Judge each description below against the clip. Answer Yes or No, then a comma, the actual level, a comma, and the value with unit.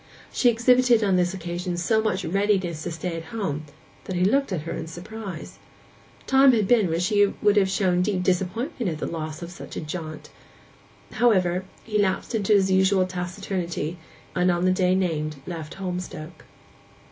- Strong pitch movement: No, average, 3.0 semitones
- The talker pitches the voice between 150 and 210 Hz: Yes, medium, 185 Hz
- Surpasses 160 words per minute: Yes, average, 175 wpm